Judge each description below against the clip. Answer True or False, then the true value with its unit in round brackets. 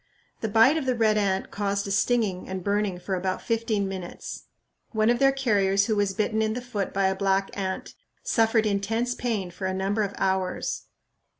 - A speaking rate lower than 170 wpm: False (195 wpm)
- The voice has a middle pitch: False (205 Hz)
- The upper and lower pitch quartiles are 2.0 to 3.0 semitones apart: True (2.7 semitones)